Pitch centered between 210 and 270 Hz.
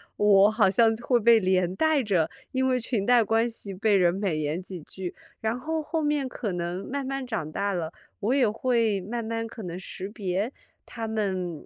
Yes: high, 215 Hz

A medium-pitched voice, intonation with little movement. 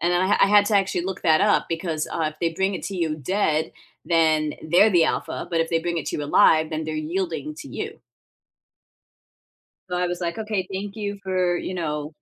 No: medium, 175 Hz; average, 3.2 semitones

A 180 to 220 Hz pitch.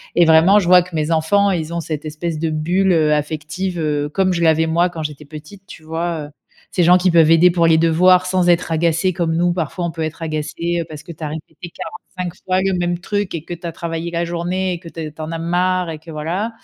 No: medium, 170 Hz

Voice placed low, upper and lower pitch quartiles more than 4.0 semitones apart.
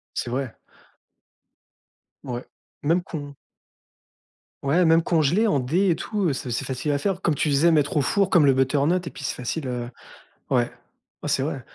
No: medium, 150 Hz; average, 4.4 semitones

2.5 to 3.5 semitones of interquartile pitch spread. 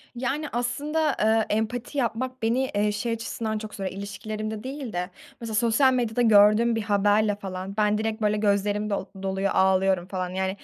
Yes: average, 2.8 semitones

